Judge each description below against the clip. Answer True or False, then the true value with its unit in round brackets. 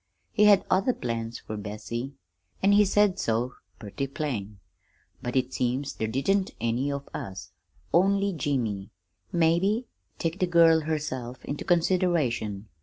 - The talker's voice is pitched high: False (140 Hz)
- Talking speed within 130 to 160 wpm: True (135 wpm)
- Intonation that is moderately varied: False (7.6 semitones)